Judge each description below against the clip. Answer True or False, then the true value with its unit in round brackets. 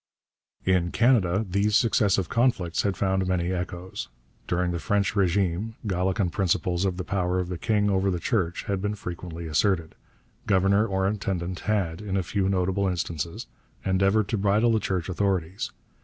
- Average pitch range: False (2.3 semitones)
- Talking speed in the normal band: True (160 wpm)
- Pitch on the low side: True (95 Hz)